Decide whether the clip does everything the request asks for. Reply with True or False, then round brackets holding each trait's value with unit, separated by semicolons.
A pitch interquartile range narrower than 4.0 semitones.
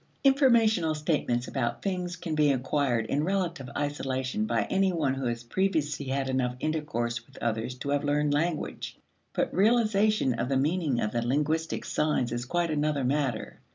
False (5.0 semitones)